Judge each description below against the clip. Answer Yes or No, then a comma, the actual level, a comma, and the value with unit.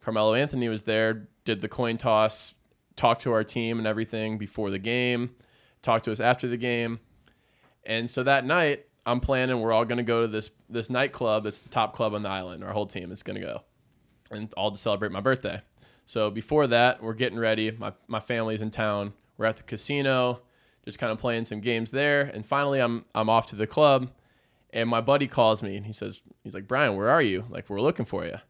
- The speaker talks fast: Yes, fast, 225 wpm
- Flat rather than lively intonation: Yes, narrow, 2.3 semitones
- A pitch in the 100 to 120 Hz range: Yes, low, 115 Hz